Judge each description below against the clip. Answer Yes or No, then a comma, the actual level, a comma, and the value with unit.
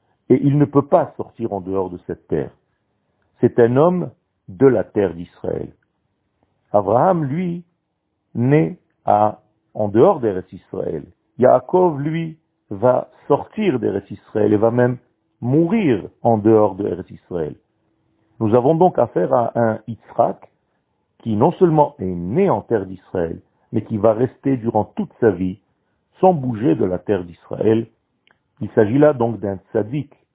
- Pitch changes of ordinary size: No, wide, 5.7 semitones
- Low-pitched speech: Yes, low, 115 Hz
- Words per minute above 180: No, average, 150 wpm